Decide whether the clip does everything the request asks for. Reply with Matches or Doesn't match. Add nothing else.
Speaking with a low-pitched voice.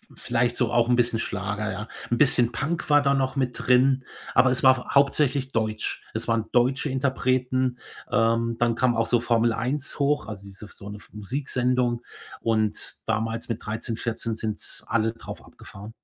Matches